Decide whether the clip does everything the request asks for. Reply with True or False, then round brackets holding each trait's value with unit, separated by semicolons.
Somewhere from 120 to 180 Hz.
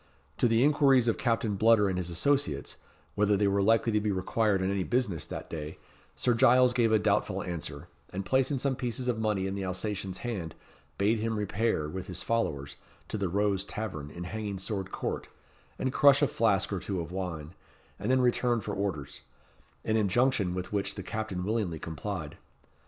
False (100 Hz)